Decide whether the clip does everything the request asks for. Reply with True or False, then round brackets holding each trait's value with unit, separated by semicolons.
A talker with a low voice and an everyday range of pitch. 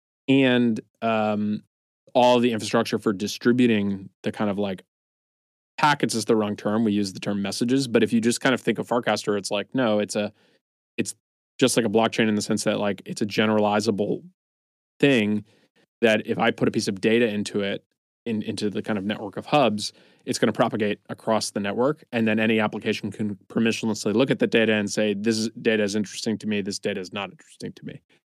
False (110 Hz; 1.7 semitones)